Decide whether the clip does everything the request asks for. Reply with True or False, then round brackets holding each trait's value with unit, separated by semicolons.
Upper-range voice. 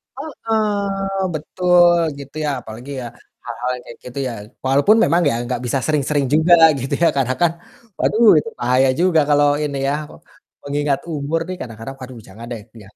False (145 Hz)